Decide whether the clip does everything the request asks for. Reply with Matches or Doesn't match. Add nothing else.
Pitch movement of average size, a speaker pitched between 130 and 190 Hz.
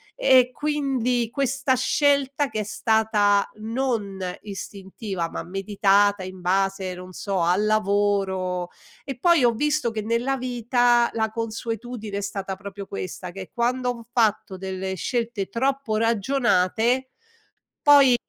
Doesn't match